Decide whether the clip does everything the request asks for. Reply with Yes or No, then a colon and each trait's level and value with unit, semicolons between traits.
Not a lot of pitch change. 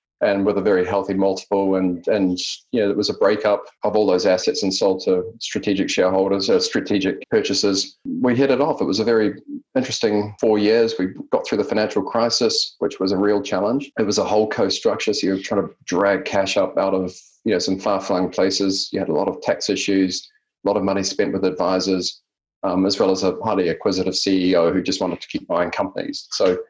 No: average, 3.2 semitones